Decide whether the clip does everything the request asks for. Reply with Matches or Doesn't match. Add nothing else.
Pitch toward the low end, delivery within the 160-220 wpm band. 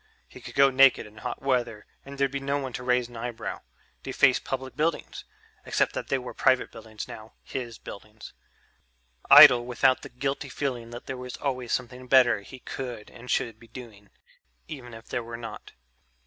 Matches